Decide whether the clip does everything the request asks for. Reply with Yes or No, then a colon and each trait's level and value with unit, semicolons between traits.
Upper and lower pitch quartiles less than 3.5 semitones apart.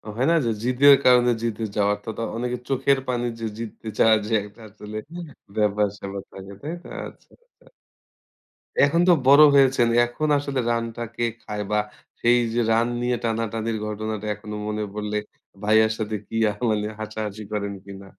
Yes: narrow, 2.6 semitones